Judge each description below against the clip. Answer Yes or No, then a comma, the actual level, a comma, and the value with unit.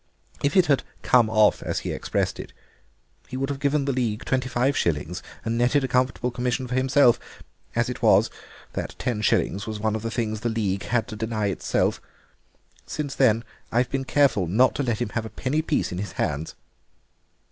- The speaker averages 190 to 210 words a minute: Yes, average, 200 wpm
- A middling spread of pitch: Yes, average, 3.5 semitones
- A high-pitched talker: No, low, 120 Hz